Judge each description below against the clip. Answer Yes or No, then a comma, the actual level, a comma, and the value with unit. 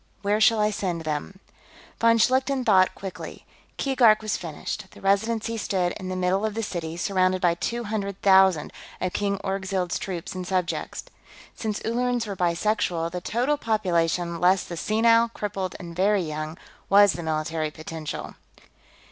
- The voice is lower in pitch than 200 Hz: Yes, high, 190 Hz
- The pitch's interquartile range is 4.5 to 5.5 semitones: No, average, 3.7 semitones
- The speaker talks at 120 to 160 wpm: Yes, average, 155 wpm